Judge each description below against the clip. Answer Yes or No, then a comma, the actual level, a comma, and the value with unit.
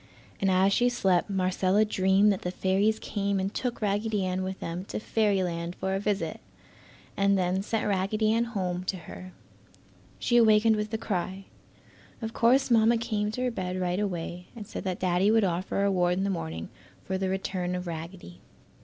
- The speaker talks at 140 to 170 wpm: No, average, 190 wpm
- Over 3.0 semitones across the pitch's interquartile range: No, average, 2.7 semitones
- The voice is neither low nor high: No, high, 195 Hz